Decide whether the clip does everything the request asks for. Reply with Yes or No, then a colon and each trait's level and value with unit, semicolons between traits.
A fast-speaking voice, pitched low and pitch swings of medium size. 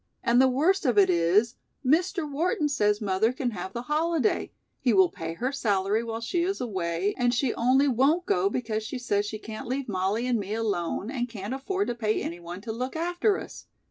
No: fast, 210 wpm; high, 235 Hz; average, 5.0 semitones